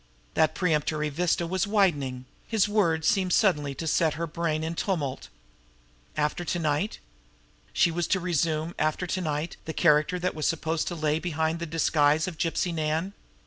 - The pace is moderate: Yes, average, 170 wpm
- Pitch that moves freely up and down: No, narrow, 2.5 semitones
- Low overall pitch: No, medium, 165 Hz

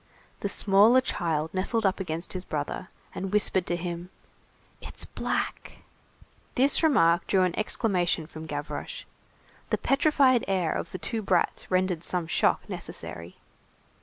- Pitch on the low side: No, medium, 185 Hz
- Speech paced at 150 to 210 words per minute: No, slow, 135 wpm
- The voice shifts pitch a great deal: No, average, 3.8 semitones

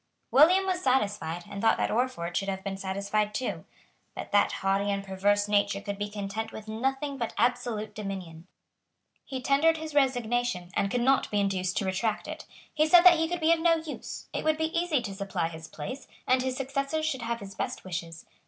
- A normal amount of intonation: No, wide, 5.8 semitones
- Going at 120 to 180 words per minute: No, fast, 205 wpm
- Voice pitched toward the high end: Yes, high, 220 Hz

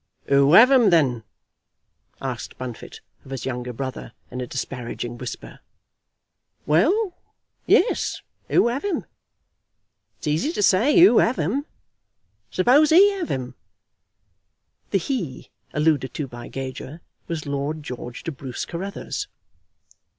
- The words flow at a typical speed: No, slow, 125 wpm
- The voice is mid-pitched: Yes, medium, 150 Hz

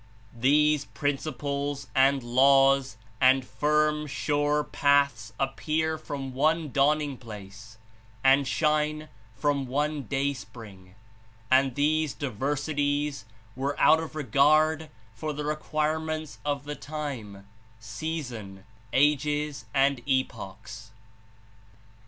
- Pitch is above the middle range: No, medium, 140 Hz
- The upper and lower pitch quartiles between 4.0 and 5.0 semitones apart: No, average, 2.8 semitones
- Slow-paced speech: Yes, slow, 100 wpm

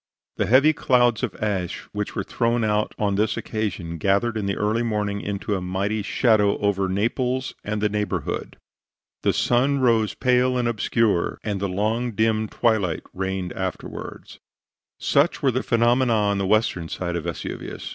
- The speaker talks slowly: No, average, 165 wpm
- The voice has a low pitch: Yes, low, 105 Hz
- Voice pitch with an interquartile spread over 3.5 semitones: No, average, 3.2 semitones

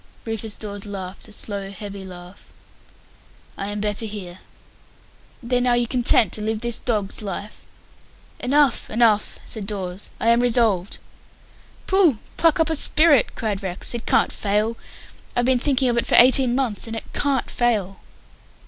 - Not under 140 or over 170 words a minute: Yes, average, 155 wpm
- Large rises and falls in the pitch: No, average, 3.3 semitones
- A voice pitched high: Yes, high, 220 Hz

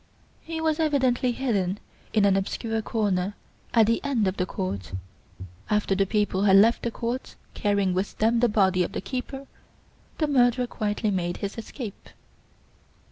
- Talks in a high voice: Yes, high, 215 Hz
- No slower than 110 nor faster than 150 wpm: No, average, 160 wpm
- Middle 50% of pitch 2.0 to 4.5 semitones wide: Yes, average, 4.0 semitones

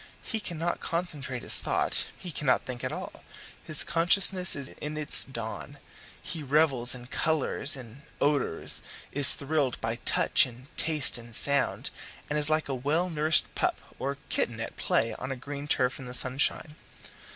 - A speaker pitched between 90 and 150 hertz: Yes, medium, 140 Hz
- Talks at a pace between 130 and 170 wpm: Yes, average, 165 wpm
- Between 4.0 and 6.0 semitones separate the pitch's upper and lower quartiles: No, average, 3.5 semitones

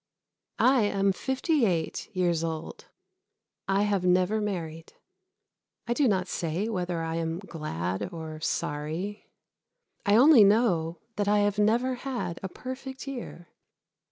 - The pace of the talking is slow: Yes, slow, 130 wpm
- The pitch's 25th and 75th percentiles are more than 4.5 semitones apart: Yes, average, 5.2 semitones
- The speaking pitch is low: No, high, 195 Hz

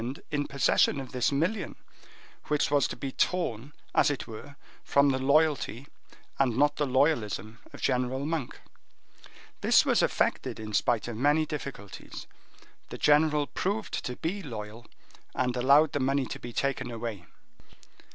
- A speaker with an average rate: Yes, average, 150 wpm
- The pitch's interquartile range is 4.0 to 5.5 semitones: No, average, 3.5 semitones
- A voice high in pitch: No, low, 135 Hz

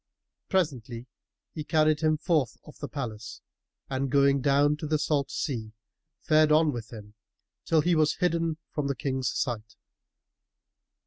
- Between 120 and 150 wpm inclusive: Yes, average, 145 wpm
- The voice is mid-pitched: Yes, medium, 145 Hz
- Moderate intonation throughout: Yes, average, 3.5 semitones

